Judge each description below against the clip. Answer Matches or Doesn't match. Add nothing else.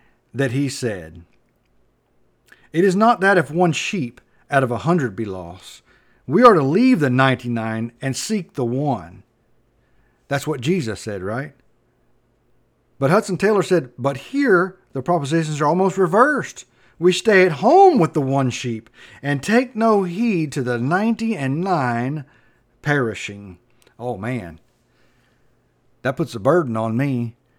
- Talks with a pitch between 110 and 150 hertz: Matches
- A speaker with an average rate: Matches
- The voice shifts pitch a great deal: Matches